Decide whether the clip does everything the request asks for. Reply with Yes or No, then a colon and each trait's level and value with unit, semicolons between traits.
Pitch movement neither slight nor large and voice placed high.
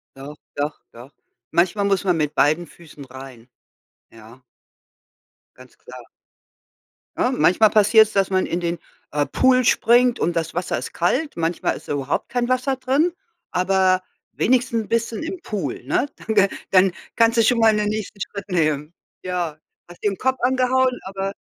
No: wide, 6.6 semitones; high, 195 Hz